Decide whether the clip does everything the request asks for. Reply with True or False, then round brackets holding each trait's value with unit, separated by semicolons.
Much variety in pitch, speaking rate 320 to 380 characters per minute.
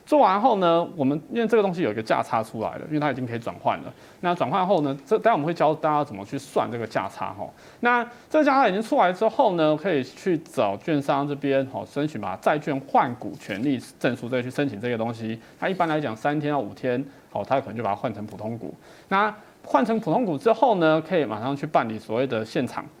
True (7.6 semitones; 355 characters per minute)